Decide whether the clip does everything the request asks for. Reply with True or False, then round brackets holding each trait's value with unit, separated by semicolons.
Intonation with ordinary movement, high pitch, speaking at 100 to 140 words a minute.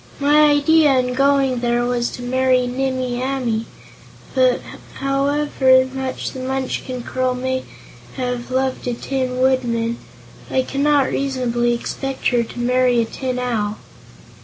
False (1.5 semitones; 255 Hz; 135 wpm)